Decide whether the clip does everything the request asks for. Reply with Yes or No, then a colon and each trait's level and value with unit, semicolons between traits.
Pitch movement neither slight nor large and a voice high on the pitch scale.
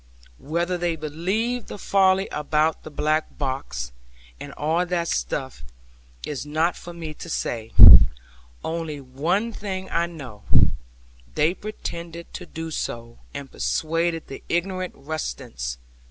No: average, 3.4 semitones; medium, 160 Hz